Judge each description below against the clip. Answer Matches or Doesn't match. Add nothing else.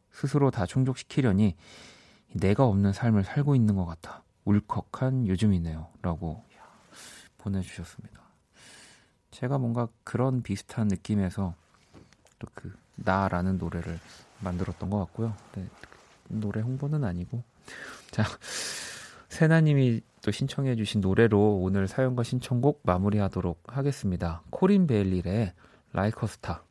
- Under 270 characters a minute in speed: Doesn't match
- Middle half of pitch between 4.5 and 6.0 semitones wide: Matches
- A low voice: Matches